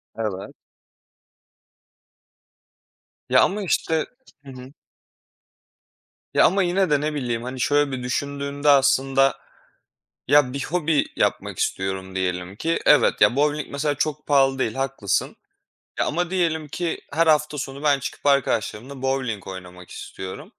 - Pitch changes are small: No, average, 3.4 semitones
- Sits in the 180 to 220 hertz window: No, medium, 140 Hz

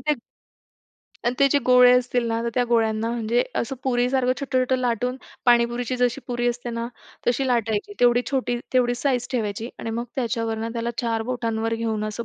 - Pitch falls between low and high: No, high, 240 Hz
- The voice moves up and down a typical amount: No, narrow, 1.5 semitones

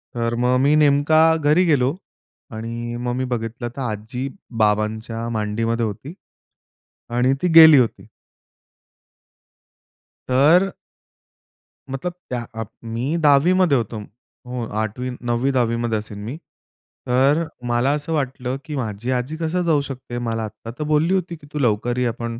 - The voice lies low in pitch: Yes, low, 125 Hz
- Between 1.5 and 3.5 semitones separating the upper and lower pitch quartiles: No, average, 4.1 semitones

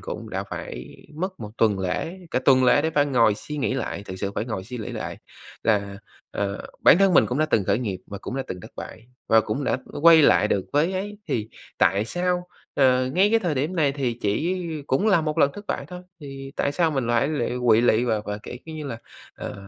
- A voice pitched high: No, low, 135 Hz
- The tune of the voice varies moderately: No, wide, 6.5 semitones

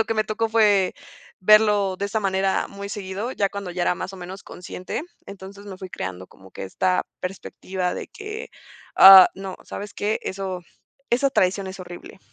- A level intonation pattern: Yes, narrow, 2.0 semitones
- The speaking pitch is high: Yes, high, 195 Hz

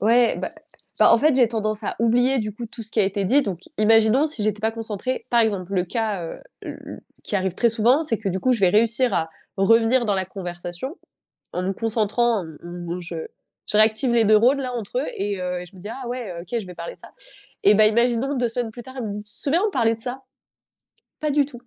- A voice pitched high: Yes, high, 220 Hz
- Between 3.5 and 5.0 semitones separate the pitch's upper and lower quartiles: Yes, average, 3.8 semitones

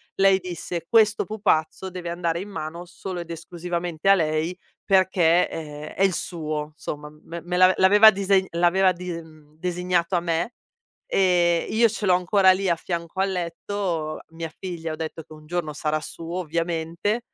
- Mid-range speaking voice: Yes, medium, 175 Hz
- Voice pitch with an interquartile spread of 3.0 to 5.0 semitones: No, narrow, 2.5 semitones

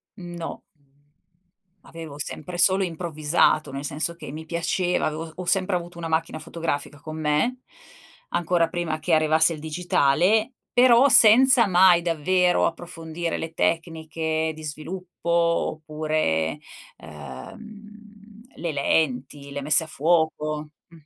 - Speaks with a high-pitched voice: No, medium, 165 Hz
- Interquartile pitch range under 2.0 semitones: No, narrow, 2.5 semitones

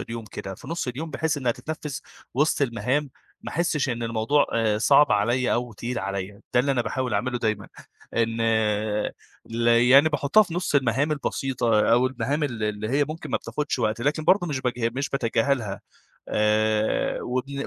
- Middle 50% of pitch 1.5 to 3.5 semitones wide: No, average, 4.0 semitones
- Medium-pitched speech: No, low, 125 Hz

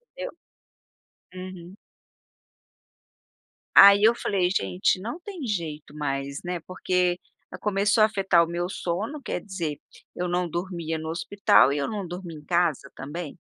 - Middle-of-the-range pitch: Yes, medium, 180 Hz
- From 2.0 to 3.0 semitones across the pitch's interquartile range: No, average, 3.4 semitones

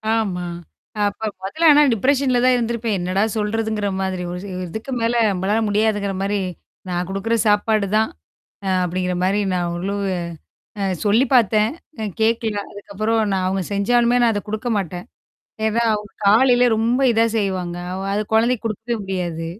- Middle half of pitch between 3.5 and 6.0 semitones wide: No, average, 3.0 semitones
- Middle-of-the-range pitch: No, high, 210 Hz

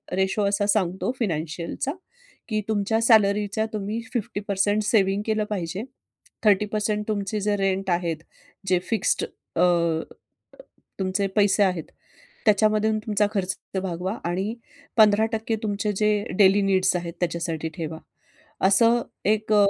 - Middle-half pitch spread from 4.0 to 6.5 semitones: No, narrow, 2.4 semitones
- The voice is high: Yes, high, 200 Hz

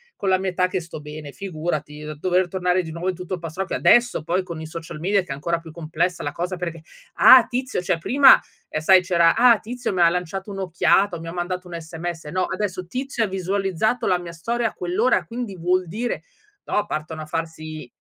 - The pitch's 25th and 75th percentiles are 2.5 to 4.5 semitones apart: Yes, average, 2.8 semitones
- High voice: No, medium, 180 Hz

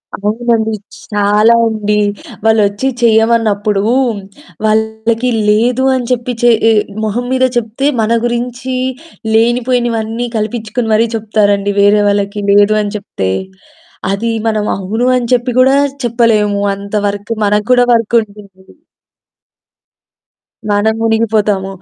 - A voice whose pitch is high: Yes, high, 220 Hz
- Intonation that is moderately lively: No, narrow, 2.3 semitones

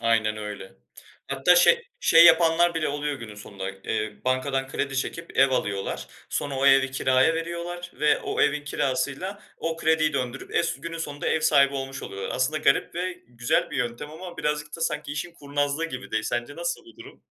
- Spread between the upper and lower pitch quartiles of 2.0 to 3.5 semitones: No, average, 4.2 semitones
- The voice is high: No, medium, 145 Hz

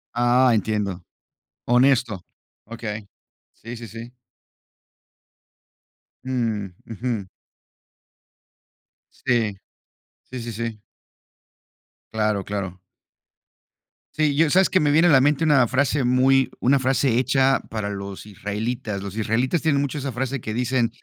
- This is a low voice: Yes, low, 120 Hz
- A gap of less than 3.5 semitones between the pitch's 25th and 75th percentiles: No, average, 3.9 semitones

